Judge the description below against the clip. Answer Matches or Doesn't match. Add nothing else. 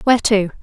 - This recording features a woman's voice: Matches